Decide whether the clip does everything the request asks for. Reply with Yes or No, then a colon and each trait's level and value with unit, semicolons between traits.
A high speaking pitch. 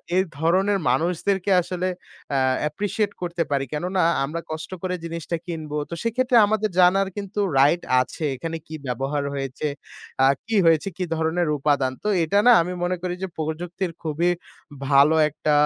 No: medium, 170 Hz